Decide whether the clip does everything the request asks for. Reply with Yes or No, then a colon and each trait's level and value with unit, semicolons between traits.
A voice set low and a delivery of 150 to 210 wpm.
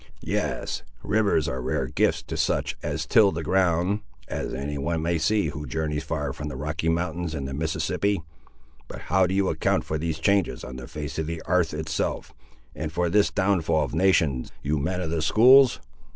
Yes: very low, 80 Hz; average, 195 wpm